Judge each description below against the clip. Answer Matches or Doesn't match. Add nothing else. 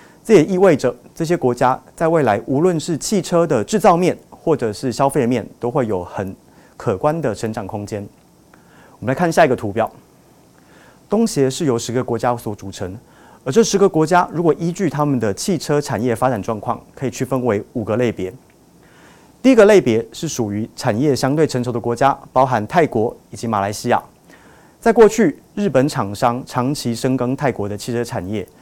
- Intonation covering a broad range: Matches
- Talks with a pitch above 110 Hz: Matches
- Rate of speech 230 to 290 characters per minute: Matches